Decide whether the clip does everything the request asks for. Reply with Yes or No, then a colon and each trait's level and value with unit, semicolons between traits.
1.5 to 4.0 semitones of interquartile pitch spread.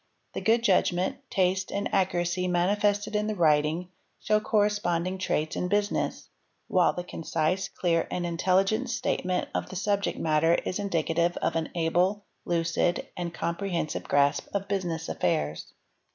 Yes: average, 3.2 semitones